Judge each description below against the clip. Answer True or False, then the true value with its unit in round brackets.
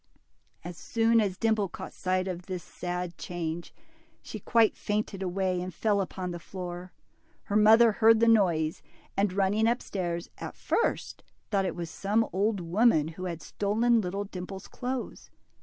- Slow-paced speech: False (160 wpm)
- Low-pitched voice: False (190 Hz)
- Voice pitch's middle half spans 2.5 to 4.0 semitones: True (3.5 semitones)